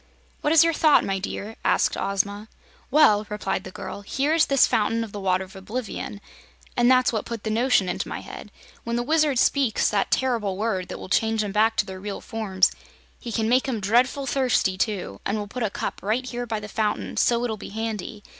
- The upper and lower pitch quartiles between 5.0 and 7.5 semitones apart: No, average, 3.5 semitones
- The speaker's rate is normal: No, fast, 220 wpm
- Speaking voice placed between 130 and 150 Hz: No, high, 220 Hz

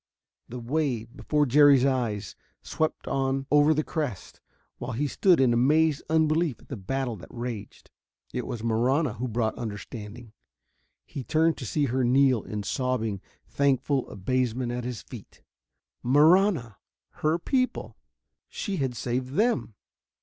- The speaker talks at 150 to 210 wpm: No, average, 140 wpm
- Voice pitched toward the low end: Yes, low, 130 Hz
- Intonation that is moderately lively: Yes, average, 4.1 semitones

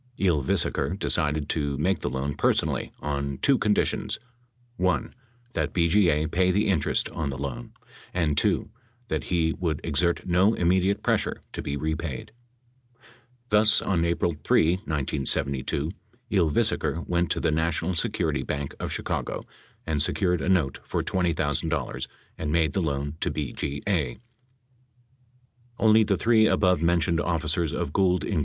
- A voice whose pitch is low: Yes, very low, 85 Hz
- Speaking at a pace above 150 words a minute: No, average, 140 wpm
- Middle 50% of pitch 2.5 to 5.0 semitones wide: Yes, average, 3.8 semitones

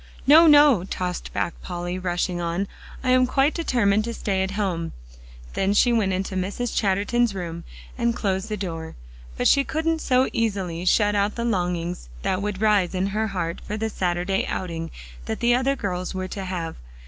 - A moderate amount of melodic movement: Yes, average, 4.4 semitones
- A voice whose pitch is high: Yes, high, 195 Hz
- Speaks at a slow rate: No, average, 185 wpm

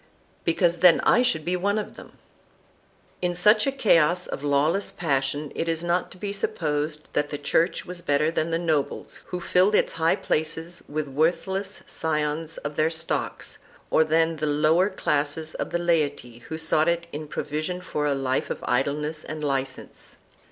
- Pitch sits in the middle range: Yes, medium, 160 Hz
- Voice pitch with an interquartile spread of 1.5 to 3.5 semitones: Yes, average, 2.8 semitones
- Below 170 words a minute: No, average, 175 wpm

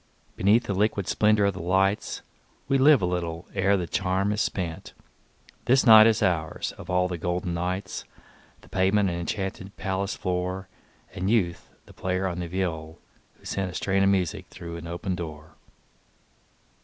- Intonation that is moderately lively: No, narrow, 2.2 semitones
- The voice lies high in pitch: No, very low, 95 Hz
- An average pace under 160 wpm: No, average, 170 wpm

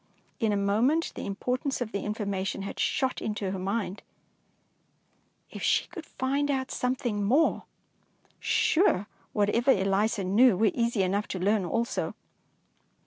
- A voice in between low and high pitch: No, high, 215 Hz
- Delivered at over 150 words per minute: No, average, 145 wpm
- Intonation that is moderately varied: Yes, average, 4.0 semitones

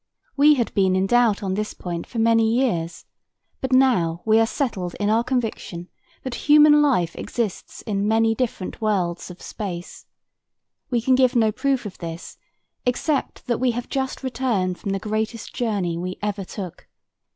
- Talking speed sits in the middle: Yes, average, 170 wpm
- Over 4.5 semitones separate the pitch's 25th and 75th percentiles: Yes, average, 5.0 semitones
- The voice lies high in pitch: Yes, high, 220 Hz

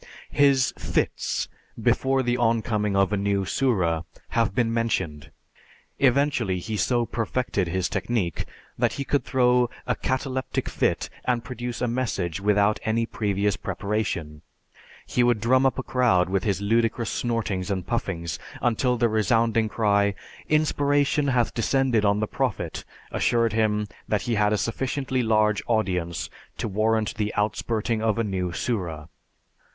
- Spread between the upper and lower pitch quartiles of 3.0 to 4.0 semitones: Yes, average, 3.3 semitones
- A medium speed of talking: Yes, average, 145 wpm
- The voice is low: Yes, low, 110 Hz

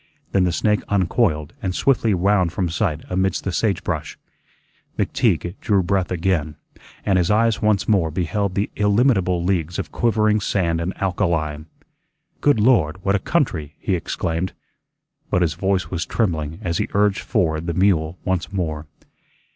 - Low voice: Yes, very low, 95 Hz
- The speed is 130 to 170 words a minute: Yes, average, 155 wpm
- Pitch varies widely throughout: No, average, 3.4 semitones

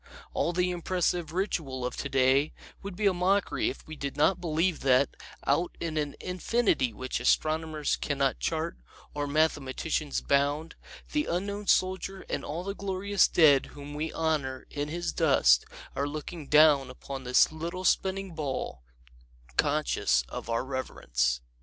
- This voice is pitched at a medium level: Yes, medium, 155 Hz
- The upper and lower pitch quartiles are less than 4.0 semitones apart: No, average, 4.4 semitones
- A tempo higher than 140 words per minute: Yes, average, 150 wpm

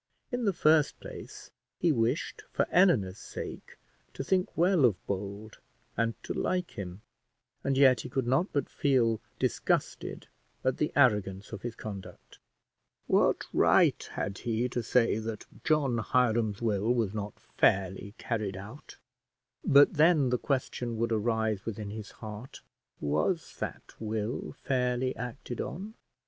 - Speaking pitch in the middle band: No, low, 115 Hz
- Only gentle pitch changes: No, average, 4.3 semitones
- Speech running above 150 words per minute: No, average, 140 wpm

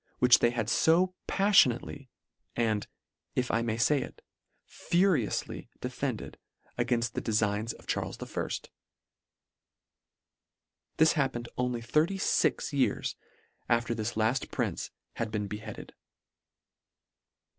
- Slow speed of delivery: Yes, slow, 110 wpm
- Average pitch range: Yes, average, 3.9 semitones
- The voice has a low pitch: Yes, low, 120 Hz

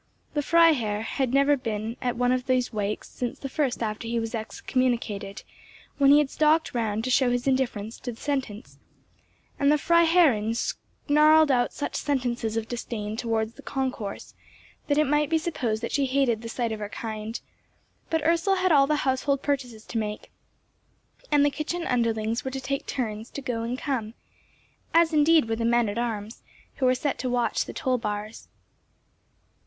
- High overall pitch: Yes, very high, 250 Hz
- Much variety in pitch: No, average, 4.2 semitones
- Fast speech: No, average, 180 wpm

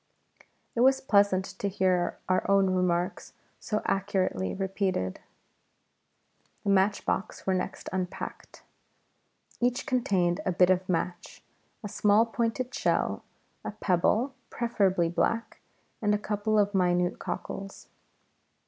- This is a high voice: Yes, high, 195 Hz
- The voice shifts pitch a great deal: No, narrow, 2.6 semitones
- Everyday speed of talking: No, slow, 115 wpm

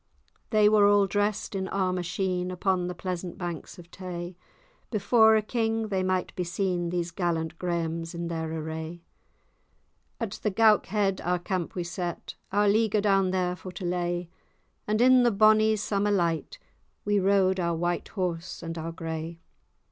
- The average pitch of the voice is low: No, medium, 185 Hz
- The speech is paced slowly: No, average, 165 wpm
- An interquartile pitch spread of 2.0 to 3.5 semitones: Yes, average, 3.0 semitones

